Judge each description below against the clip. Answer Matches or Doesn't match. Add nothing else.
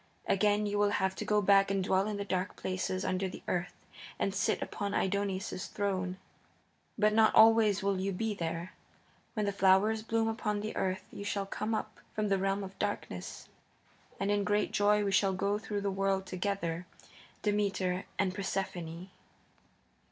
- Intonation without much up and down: Matches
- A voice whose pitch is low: Doesn't match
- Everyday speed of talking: Matches